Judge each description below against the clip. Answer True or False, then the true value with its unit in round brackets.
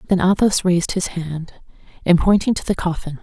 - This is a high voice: False (180 Hz)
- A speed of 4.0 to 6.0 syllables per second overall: True (5.4 syllables/s)